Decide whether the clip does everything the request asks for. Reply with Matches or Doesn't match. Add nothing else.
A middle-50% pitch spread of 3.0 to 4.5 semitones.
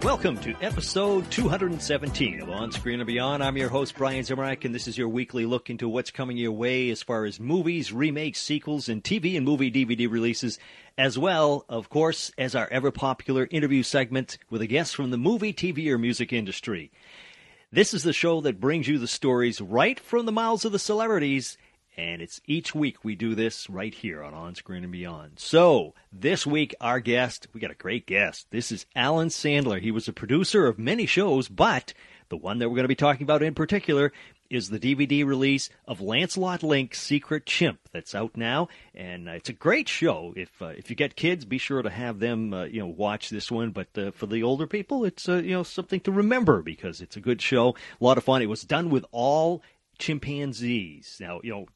Doesn't match